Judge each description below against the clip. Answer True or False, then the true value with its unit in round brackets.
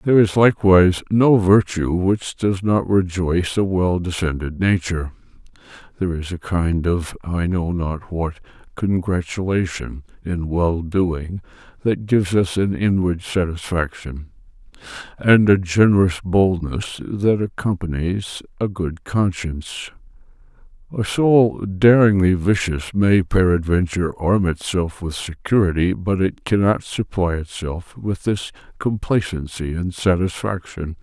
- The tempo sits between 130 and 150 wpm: False (120 wpm)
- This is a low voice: True (90 Hz)